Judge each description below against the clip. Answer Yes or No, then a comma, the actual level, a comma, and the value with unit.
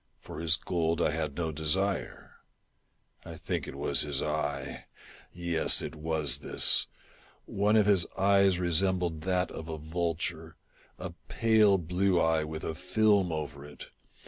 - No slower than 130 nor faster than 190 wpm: Yes, average, 155 wpm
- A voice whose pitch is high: No, very low, 85 Hz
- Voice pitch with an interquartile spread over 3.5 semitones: No, average, 3.2 semitones